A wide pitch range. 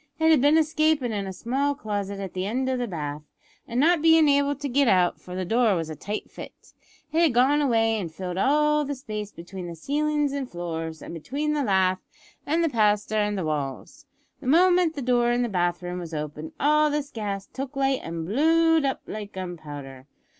Yes: wide, 8.0 semitones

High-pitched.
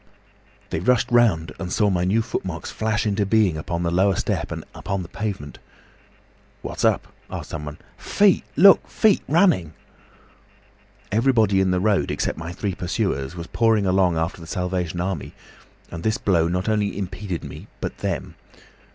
No: very low, 95 Hz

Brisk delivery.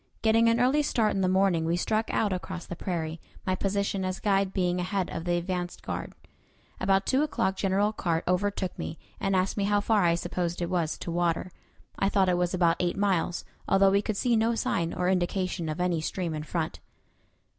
Yes: fast, 210 wpm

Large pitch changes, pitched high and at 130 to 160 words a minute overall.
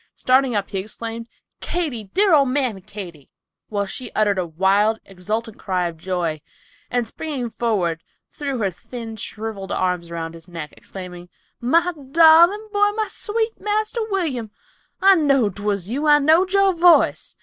Yes: wide, 8.8 semitones; high, 230 Hz; average, 155 wpm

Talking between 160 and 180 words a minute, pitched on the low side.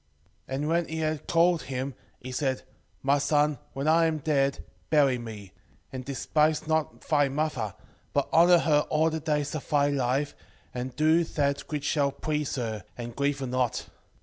No: average, 175 wpm; medium, 145 Hz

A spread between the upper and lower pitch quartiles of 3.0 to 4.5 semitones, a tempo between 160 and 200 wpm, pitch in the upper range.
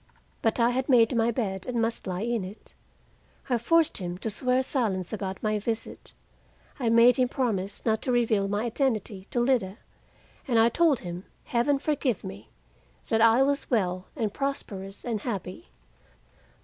Yes: average, 4.1 semitones; average, 165 wpm; high, 230 Hz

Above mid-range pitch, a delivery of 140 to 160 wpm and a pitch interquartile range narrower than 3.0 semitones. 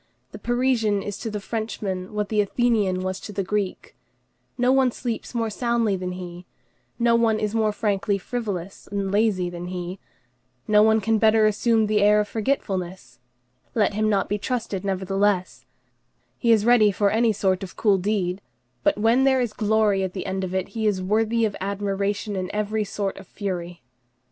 No: high, 205 Hz; average, 185 wpm; narrow, 2.5 semitones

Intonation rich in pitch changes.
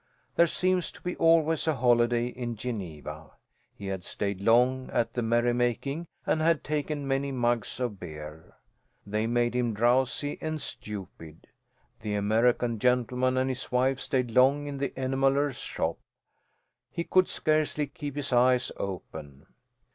No: average, 3.9 semitones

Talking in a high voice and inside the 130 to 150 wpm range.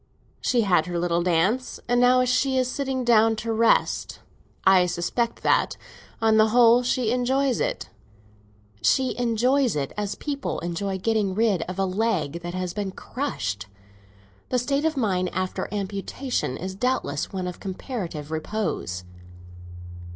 Yes: high, 215 Hz; average, 145 wpm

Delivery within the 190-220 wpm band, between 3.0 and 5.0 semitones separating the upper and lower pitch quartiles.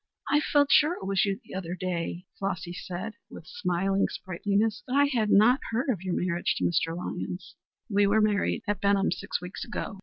Yes: average, 200 wpm; average, 3.3 semitones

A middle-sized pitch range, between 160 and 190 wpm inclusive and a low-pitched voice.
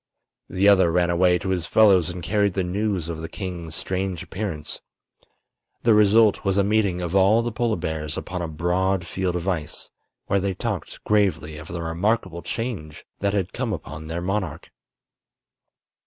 Yes: average, 3.1 semitones; average, 170 wpm; very low, 95 Hz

